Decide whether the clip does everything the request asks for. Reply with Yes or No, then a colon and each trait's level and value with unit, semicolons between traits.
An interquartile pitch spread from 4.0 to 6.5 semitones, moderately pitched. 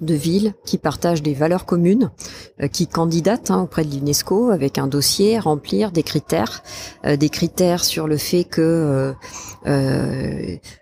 Yes: average, 4.3 semitones; medium, 160 Hz